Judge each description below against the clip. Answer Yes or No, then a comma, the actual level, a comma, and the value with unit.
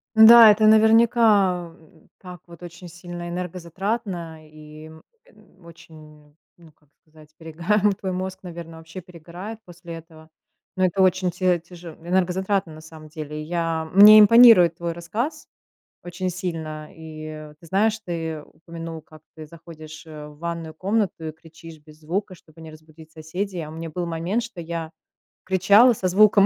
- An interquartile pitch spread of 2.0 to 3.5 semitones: Yes, average, 2.9 semitones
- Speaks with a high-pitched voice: No, medium, 170 Hz